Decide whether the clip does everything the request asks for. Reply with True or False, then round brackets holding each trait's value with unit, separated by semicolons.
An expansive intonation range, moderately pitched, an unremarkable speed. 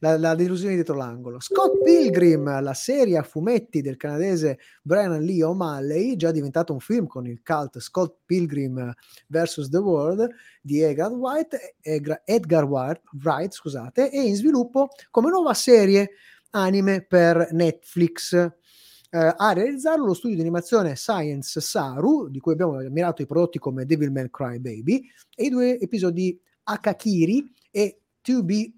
True (5.7 semitones; 170 Hz; 150 wpm)